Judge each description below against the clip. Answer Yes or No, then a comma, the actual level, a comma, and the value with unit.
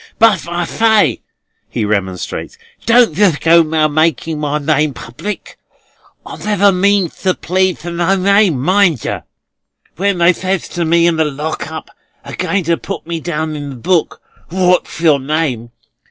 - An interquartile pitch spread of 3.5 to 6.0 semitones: Yes, average, 3.8 semitones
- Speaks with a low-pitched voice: No, medium, 170 Hz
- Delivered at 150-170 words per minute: Yes, average, 165 wpm